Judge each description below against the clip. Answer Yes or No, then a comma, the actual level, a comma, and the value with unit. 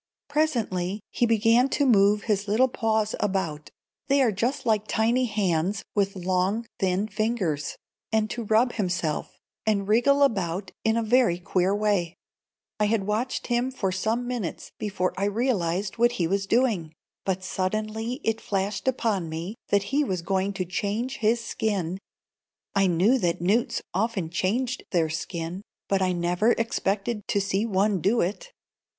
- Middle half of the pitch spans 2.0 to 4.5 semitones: Yes, average, 3.6 semitones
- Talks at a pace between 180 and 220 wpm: No, average, 155 wpm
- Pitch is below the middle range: No, high, 205 Hz